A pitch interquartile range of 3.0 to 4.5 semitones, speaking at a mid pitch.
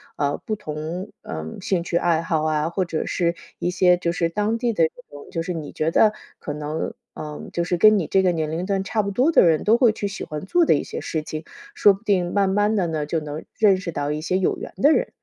Yes: average, 4.2 semitones; medium, 175 Hz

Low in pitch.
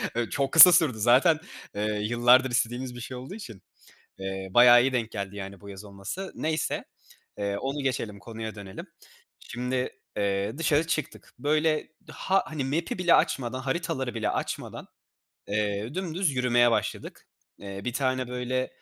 Yes: low, 125 Hz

